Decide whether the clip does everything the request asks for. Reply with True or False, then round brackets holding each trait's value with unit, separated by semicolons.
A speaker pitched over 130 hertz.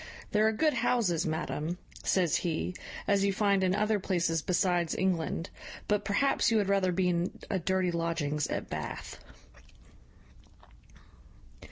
True (185 Hz)